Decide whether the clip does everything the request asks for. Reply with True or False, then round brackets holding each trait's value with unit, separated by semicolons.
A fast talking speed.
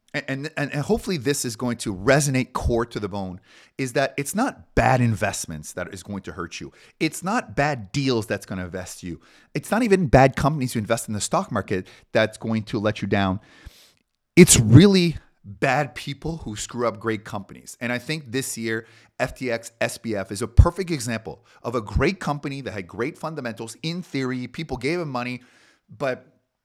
False (195 wpm)